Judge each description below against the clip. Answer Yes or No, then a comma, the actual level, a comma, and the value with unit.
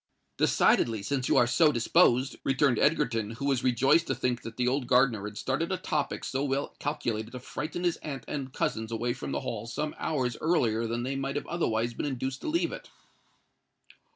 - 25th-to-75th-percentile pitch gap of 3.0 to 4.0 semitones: Yes, average, 3.6 semitones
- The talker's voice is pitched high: No, low, 130 Hz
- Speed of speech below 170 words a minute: No, average, 195 wpm